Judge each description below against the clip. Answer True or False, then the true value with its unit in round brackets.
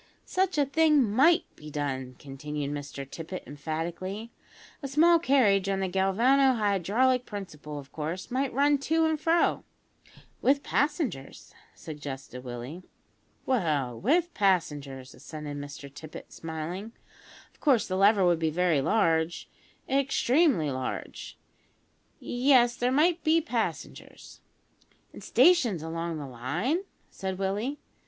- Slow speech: True (125 wpm)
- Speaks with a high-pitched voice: True (195 Hz)